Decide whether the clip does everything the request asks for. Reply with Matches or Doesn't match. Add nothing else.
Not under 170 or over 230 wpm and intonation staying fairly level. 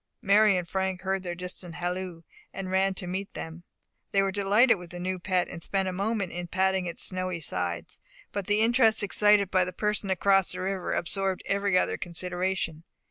Matches